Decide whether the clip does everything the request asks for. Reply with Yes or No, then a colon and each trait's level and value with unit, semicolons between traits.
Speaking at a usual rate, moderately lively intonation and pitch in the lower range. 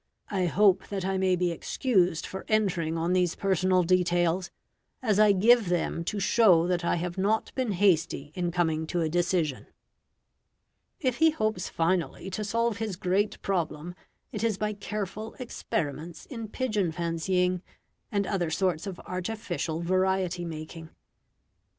No: average, 150 wpm; average, 3.2 semitones; medium, 185 Hz